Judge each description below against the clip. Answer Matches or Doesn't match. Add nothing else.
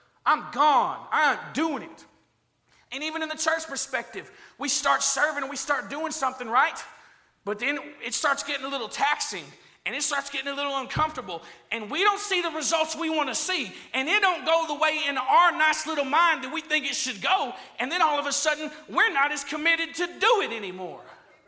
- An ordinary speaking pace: Doesn't match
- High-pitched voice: Matches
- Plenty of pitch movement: Doesn't match